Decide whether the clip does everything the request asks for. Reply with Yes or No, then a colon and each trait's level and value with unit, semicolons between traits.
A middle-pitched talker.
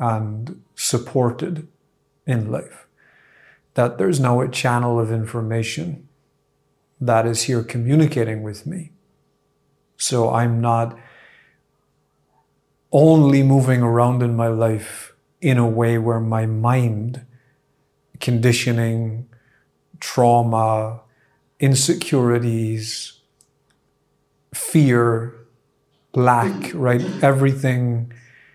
No: low, 120 Hz